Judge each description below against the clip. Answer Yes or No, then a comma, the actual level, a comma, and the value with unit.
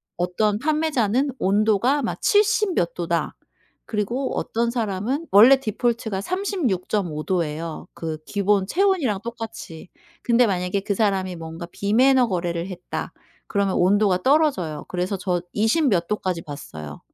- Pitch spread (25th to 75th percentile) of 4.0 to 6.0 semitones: Yes, wide, 5.6 semitones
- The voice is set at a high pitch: Yes, high, 205 Hz